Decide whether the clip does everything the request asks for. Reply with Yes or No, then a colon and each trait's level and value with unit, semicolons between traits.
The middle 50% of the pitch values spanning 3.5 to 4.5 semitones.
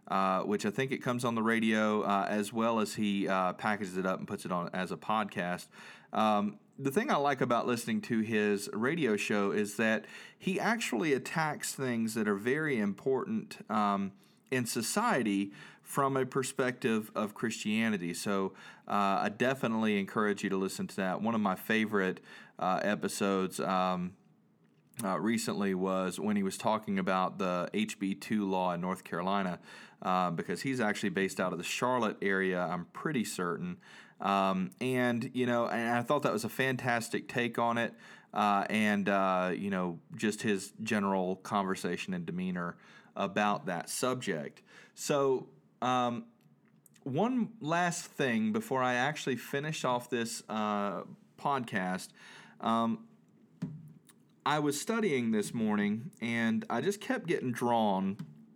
No: average, 5.3 semitones